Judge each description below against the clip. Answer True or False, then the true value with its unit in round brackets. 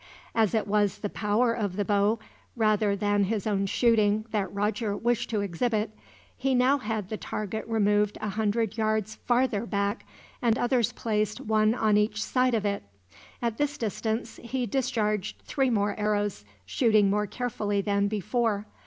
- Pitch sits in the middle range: False (215 Hz)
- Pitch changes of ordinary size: False (2.0 semitones)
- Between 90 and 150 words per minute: False (160 wpm)